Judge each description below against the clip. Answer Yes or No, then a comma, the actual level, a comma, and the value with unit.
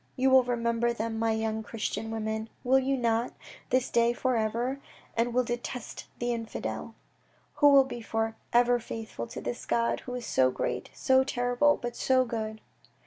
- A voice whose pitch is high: Yes, high, 235 Hz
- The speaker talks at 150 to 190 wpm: Yes, average, 175 wpm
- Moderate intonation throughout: No, narrow, 2.0 semitones